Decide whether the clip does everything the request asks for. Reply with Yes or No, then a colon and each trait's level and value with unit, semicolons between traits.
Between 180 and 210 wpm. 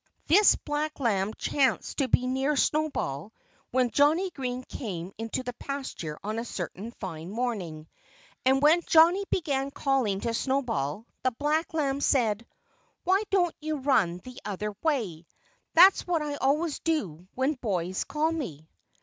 No: average, 150 wpm